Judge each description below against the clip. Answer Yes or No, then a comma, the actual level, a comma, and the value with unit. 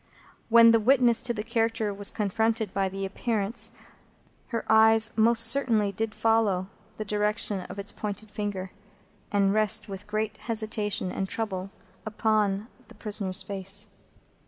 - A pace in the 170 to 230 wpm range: No, slow, 135 wpm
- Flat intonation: Yes, narrow, 2.0 semitones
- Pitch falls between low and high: No, high, 215 Hz